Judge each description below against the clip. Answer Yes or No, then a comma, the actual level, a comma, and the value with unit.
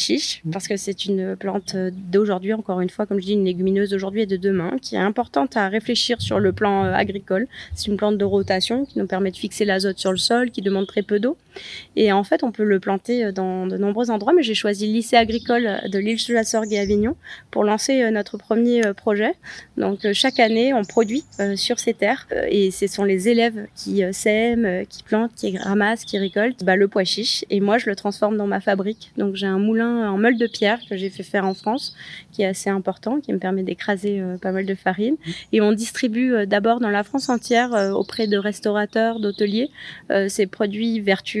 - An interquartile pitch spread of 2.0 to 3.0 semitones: Yes, narrow, 2.6 semitones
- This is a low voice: No, high, 210 Hz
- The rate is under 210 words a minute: No, average, 215 wpm